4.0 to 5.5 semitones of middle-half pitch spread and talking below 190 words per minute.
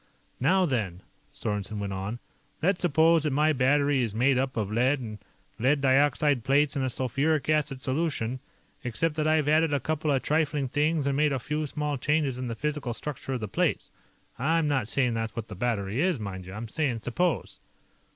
No: average, 4.4 semitones; average, 195 wpm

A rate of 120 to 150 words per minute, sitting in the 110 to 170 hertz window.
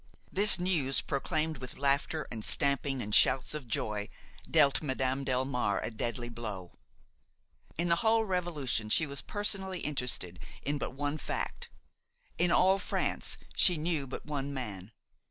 Yes: average, 145 wpm; medium, 140 Hz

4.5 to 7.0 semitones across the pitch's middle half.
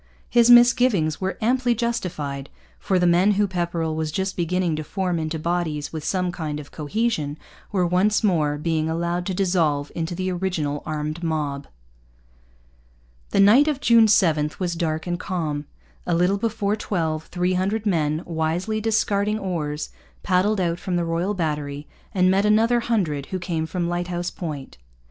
No: average, 4.0 semitones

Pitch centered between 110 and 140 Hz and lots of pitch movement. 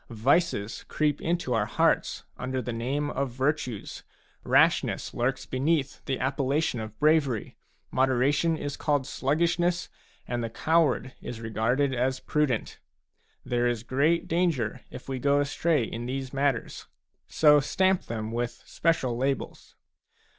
No: low, 135 Hz; average, 3.6 semitones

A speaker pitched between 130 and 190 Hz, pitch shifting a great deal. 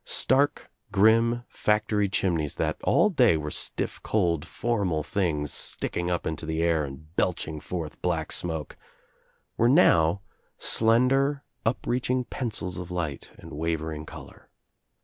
No: very low, 90 Hz; wide, 6.4 semitones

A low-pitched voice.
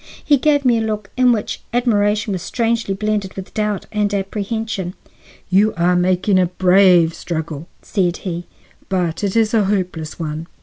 No: high, 195 Hz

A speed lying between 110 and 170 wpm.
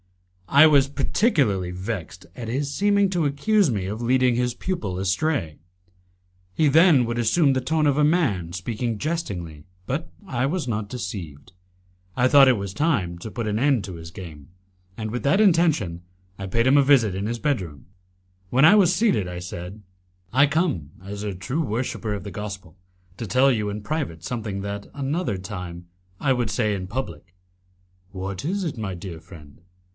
No: average, 180 wpm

